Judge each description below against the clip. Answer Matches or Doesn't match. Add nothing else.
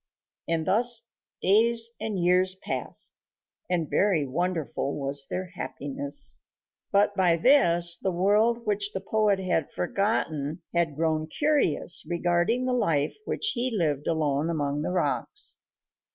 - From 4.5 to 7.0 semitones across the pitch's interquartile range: Matches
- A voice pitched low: Doesn't match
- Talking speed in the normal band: Doesn't match